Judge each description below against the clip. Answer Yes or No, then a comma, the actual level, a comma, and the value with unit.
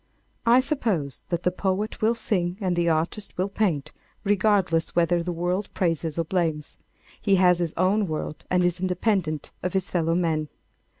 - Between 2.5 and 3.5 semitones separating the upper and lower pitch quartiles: Yes, average, 3.0 semitones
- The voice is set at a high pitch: No, medium, 180 Hz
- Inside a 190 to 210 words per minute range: No, average, 170 wpm